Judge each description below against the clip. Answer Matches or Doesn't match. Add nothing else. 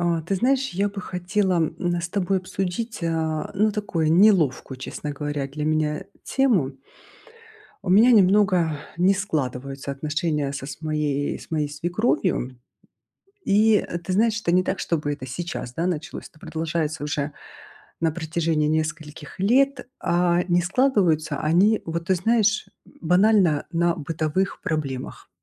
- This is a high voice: Doesn't match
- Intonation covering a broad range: Doesn't match